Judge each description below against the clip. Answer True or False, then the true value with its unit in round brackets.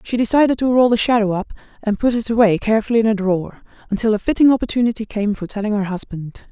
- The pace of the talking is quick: True (220 wpm)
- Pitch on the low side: False (220 Hz)